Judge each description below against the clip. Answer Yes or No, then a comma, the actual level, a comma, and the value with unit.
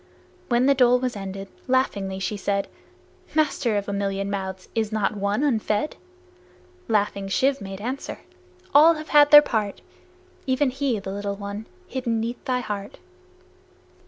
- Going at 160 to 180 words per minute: No, average, 150 wpm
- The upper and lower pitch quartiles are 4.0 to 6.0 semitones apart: Yes, average, 4.5 semitones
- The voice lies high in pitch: Yes, high, 215 Hz